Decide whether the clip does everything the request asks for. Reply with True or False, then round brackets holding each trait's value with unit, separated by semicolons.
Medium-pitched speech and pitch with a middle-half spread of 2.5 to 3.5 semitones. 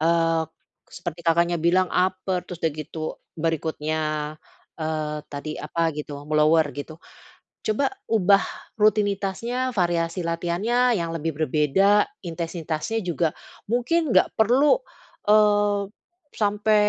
False (170 Hz; 4.7 semitones)